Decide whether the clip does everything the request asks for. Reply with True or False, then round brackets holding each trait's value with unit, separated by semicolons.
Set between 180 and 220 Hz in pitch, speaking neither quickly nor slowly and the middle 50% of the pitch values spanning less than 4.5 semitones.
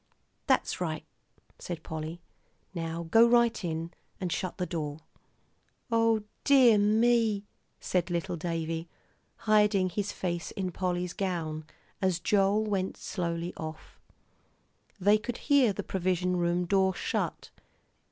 False (185 Hz; 125 wpm; 3.7 semitones)